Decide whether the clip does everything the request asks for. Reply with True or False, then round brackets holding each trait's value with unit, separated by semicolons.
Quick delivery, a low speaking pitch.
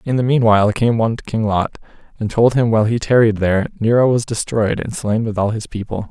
True (235 wpm; 110 Hz)